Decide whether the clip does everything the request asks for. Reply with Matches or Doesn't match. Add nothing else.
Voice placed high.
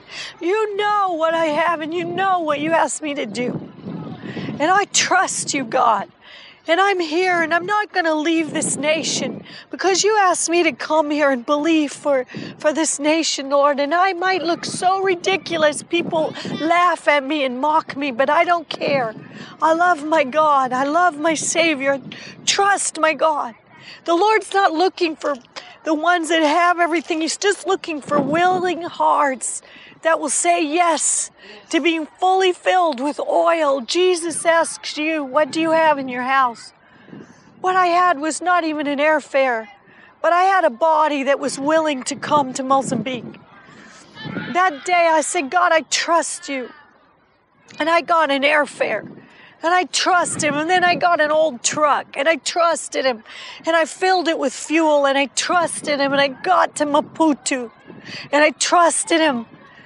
Matches